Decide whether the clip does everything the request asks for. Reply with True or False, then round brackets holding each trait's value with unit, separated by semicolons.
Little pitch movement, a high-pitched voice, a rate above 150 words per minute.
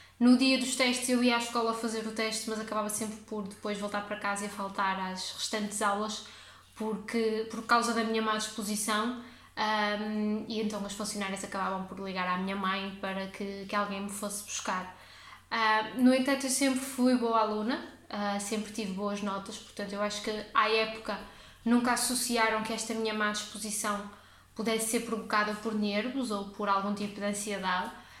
True (1.8 semitones; 215 Hz; 185 wpm)